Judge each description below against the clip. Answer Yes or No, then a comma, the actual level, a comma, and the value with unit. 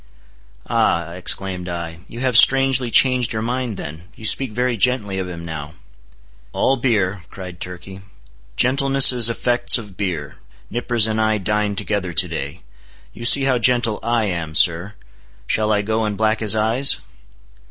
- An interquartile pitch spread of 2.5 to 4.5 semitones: No, average, 4.9 semitones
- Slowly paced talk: No, average, 155 wpm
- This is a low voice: Yes, low, 110 Hz